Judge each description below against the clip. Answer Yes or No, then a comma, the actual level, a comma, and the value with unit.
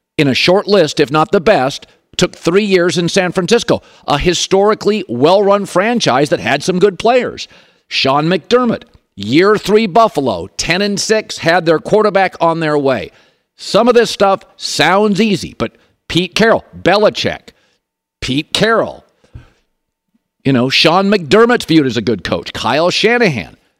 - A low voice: No, medium, 185 Hz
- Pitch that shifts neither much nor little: Yes, average, 4.9 semitones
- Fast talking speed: No, average, 150 wpm